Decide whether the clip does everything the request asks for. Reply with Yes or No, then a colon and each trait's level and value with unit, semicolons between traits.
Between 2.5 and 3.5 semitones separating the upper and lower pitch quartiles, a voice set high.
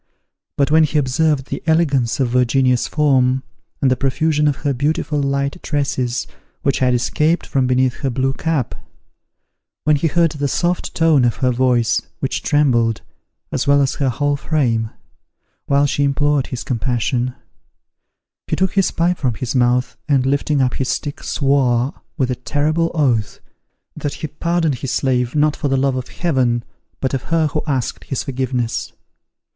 No: average, 2.8 semitones; low, 135 Hz